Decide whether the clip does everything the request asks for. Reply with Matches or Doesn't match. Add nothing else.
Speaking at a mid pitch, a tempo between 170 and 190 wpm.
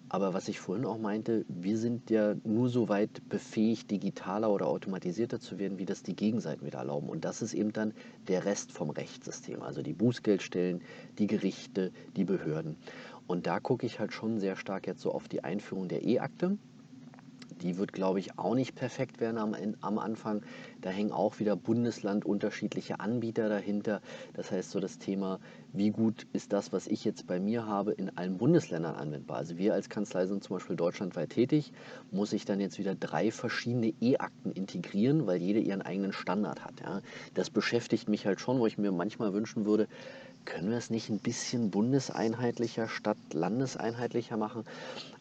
Doesn't match